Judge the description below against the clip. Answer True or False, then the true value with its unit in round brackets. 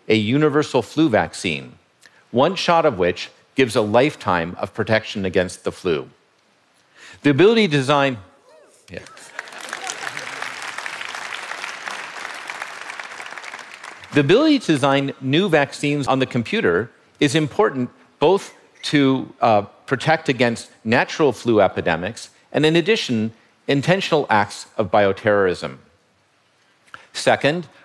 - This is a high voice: False (140 Hz)